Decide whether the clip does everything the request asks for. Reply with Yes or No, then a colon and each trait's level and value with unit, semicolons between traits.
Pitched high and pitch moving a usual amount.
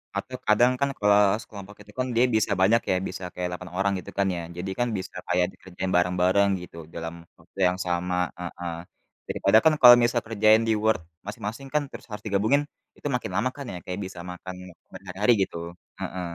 No: low, 100 Hz; average, 3.5 semitones